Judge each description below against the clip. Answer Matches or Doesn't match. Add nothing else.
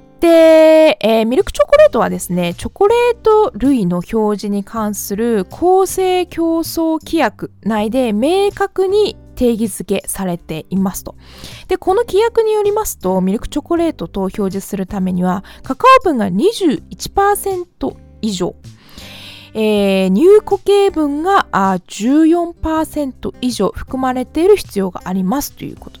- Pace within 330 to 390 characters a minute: Doesn't match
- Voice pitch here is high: Matches